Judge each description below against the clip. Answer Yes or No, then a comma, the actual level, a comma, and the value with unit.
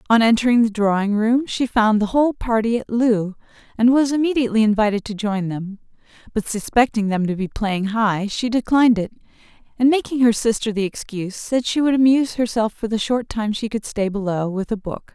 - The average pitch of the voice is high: Yes, high, 225 Hz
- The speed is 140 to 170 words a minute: No, average, 200 wpm